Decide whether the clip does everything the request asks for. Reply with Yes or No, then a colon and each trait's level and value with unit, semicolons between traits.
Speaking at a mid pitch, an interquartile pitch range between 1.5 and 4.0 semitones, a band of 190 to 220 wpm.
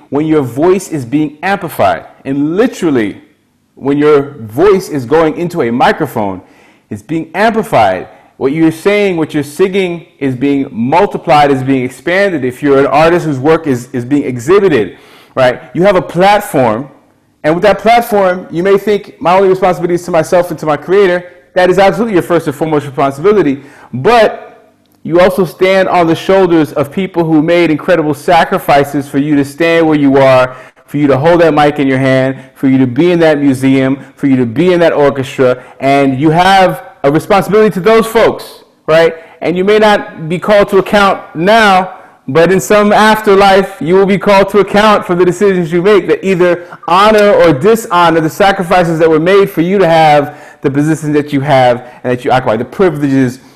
No: medium, 165 Hz; average, 5.2 semitones; average, 195 wpm